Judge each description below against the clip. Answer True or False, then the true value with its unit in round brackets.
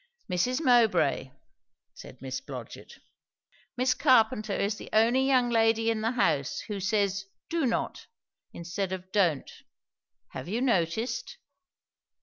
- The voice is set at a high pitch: True (225 Hz)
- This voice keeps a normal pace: False (125 wpm)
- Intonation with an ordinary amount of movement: True (4.2 semitones)